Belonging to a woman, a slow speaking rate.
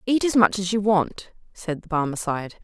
No: female; fast, 205 wpm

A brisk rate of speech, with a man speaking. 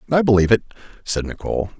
No: average, 165 wpm; male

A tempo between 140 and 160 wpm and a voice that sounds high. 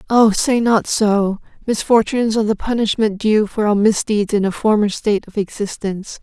No: average, 175 wpm; high, 210 Hz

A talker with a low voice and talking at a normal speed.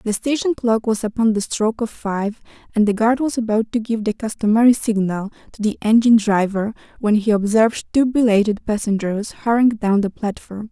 No: high, 220 Hz; average, 185 wpm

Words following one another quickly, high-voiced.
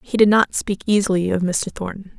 Yes: fast, 220 wpm; high, 195 Hz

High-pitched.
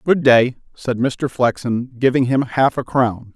No: low, 125 Hz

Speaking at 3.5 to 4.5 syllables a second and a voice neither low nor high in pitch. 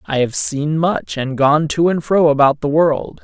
Yes: 4.2 syllables/s; medium, 150 Hz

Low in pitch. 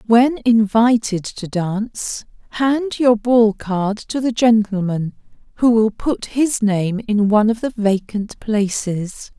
No: high, 220 Hz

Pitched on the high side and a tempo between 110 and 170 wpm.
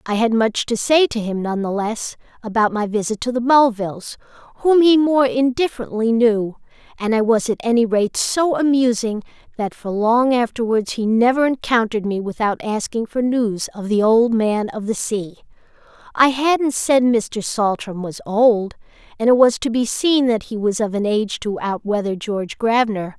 No: high, 225 Hz; average, 185 wpm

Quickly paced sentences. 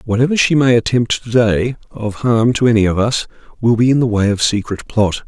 Yes: fast, 230 wpm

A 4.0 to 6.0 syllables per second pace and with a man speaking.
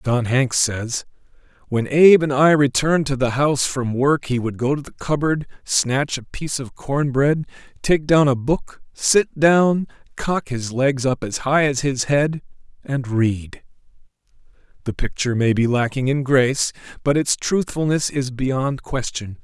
Yes: 4.3 syllables/s; male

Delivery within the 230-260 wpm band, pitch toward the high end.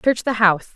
Yes: fast, 240 wpm; high, 215 Hz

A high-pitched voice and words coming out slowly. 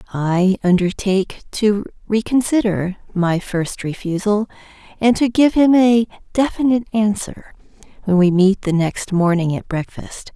Yes: high, 205 Hz; slow, 130 wpm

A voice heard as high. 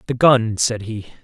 No: low, 110 Hz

